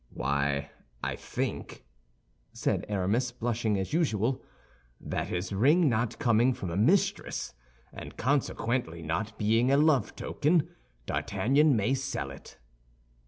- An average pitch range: No, wide, 5.7 semitones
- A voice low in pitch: Yes, low, 115 Hz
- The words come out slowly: Yes, slow, 120 wpm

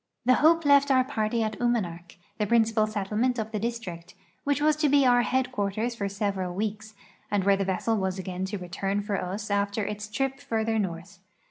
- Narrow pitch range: No, average, 3.6 semitones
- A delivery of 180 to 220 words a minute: Yes, average, 195 wpm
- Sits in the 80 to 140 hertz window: No, high, 215 Hz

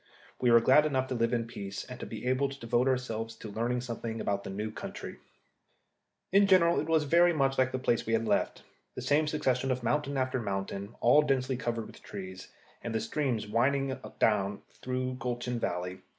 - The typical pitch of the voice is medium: No, low, 125 Hz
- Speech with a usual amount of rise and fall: Yes, average, 3.3 semitones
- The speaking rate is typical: No, fast, 210 wpm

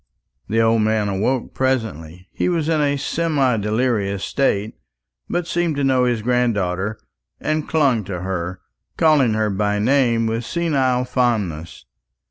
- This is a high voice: No, low, 115 Hz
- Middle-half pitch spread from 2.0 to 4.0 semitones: No, average, 4.9 semitones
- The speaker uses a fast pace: No, average, 140 wpm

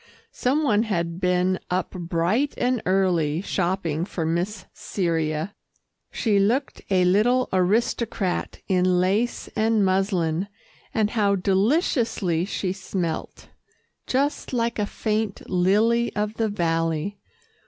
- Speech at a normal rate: No, slow, 115 wpm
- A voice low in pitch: No, high, 195 Hz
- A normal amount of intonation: Yes, average, 3.7 semitones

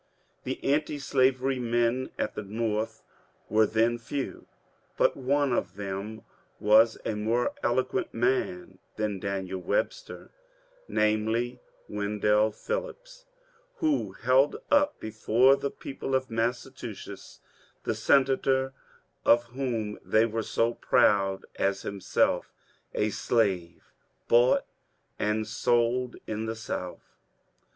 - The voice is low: Yes, low, 115 Hz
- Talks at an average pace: No, slow, 110 wpm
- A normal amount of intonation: Yes, average, 3.8 semitones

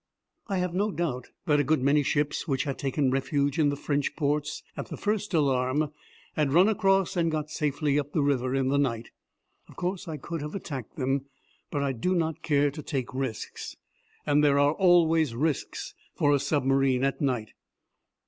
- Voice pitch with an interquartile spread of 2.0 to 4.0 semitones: Yes, average, 3.0 semitones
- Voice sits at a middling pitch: Yes, medium, 145 Hz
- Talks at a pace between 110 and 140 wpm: No, average, 190 wpm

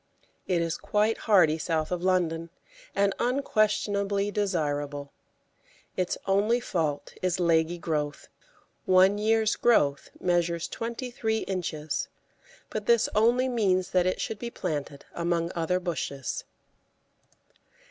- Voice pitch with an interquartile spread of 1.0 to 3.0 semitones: No, average, 4.4 semitones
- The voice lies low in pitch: No, medium, 185 Hz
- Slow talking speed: Yes, slow, 115 wpm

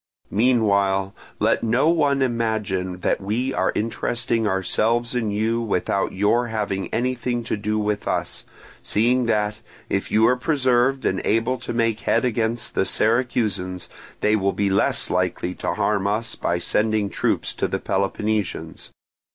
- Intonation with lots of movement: No, average, 3.2 semitones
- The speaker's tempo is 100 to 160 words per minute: Yes, average, 150 wpm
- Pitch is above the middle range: No, low, 110 Hz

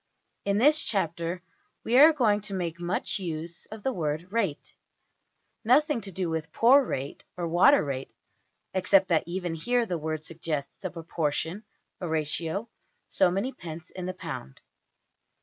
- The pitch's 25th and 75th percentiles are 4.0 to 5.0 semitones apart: Yes, average, 4.6 semitones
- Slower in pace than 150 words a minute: No, average, 155 wpm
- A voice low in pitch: No, medium, 180 Hz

